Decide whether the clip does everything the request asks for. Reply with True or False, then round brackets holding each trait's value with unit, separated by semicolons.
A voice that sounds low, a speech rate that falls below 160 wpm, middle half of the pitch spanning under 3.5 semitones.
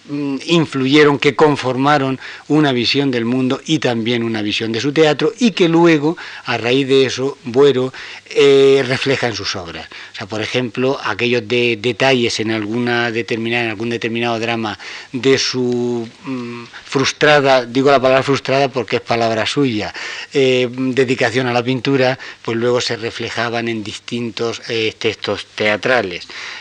True (125 Hz; 150 wpm; 2.7 semitones)